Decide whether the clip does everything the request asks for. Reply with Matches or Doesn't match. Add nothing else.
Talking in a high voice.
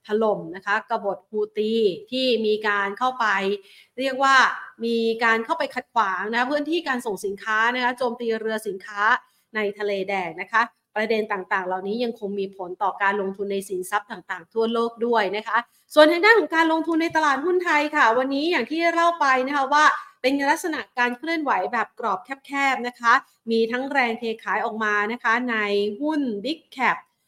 Matches